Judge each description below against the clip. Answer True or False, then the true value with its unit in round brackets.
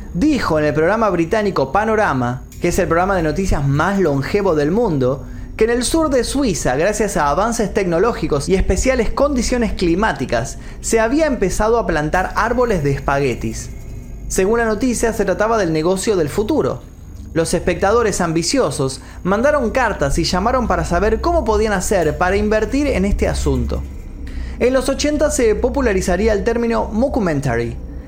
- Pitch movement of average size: False (7.6 semitones)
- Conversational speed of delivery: True (155 wpm)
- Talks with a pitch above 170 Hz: True (190 Hz)